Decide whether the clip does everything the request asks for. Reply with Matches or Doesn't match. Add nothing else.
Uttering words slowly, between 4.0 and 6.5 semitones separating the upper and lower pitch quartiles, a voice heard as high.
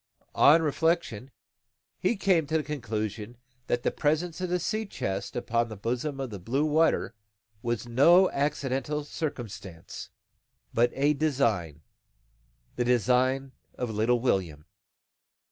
Doesn't match